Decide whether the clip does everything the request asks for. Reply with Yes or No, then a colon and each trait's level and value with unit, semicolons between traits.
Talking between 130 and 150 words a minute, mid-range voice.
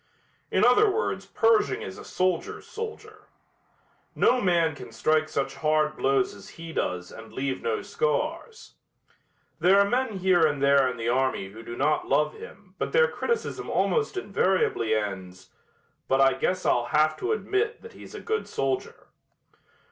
No: average, 165 wpm; medium, 160 Hz